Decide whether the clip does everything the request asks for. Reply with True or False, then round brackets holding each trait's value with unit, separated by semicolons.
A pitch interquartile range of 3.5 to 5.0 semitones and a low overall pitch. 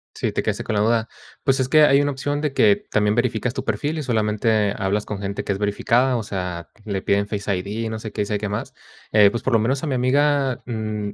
True (4.2 semitones; 110 Hz)